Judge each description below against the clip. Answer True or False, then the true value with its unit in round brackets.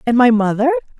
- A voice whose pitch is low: False (230 Hz)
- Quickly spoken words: False (180 wpm)